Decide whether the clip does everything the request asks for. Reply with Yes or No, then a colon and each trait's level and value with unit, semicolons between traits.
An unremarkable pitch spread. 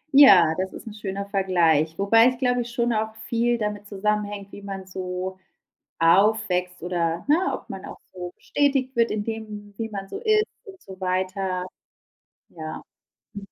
Yes: average, 3.6 semitones